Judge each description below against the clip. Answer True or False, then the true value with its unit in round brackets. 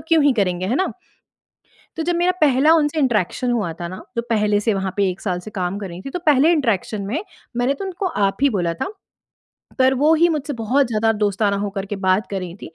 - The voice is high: True (225 Hz)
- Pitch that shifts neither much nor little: False (6.8 semitones)